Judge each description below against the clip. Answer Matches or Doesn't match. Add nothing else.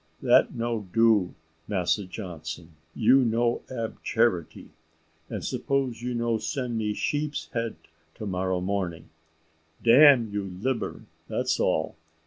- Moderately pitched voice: Doesn't match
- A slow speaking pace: Matches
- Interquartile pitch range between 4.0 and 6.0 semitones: Matches